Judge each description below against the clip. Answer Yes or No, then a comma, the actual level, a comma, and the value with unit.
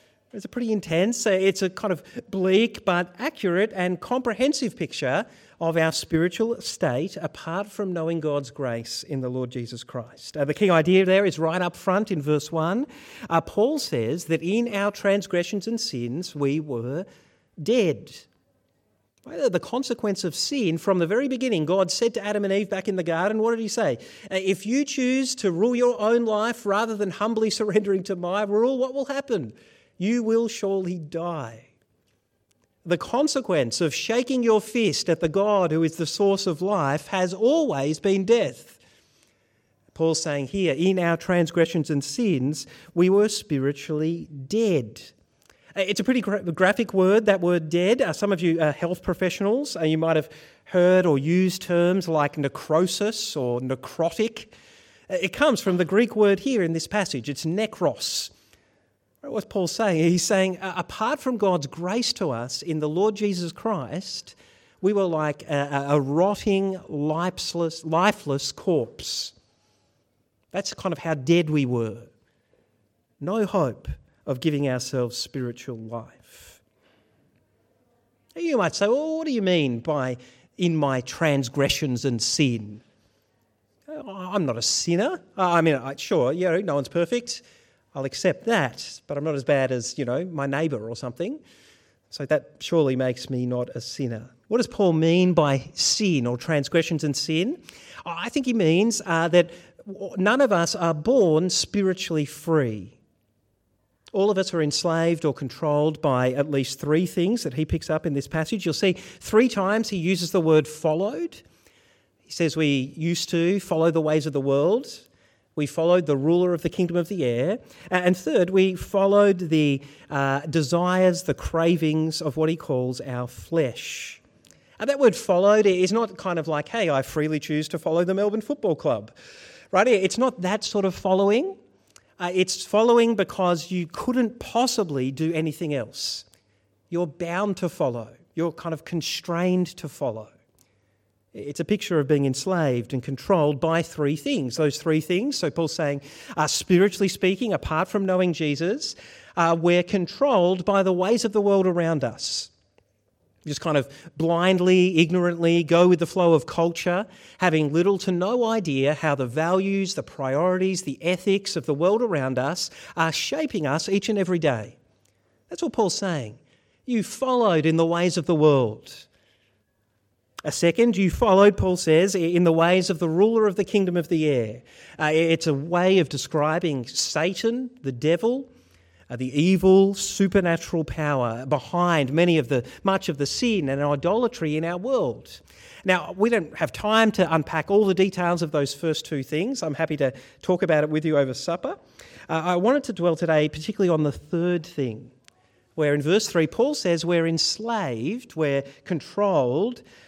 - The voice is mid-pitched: Yes, medium, 170 Hz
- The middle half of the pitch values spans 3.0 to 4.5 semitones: No, average, 5.2 semitones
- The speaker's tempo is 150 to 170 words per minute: Yes, average, 165 wpm